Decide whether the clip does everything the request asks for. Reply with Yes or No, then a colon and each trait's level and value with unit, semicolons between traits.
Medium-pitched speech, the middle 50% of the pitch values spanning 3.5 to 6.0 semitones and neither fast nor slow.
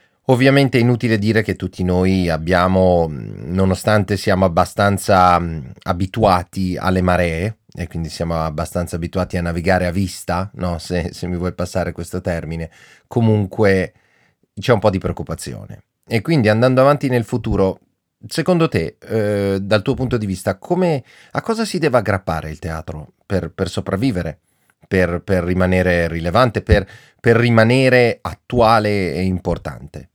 No: very low, 95 Hz; average, 4.0 semitones; average, 145 wpm